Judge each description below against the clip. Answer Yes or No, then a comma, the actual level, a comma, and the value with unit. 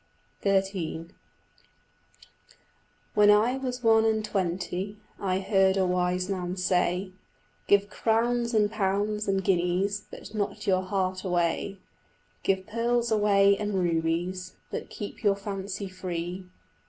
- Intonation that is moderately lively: No, narrow, 2.3 semitones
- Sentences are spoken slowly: Yes, slow, 120 wpm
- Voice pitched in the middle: No, high, 195 Hz